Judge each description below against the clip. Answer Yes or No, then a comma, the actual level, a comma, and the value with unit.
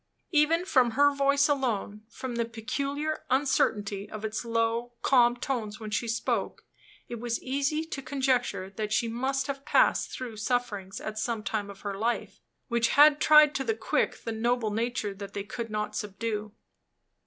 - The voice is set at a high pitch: Yes, high, 235 Hz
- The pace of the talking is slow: No, average, 170 wpm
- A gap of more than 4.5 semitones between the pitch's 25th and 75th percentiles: No, average, 4.1 semitones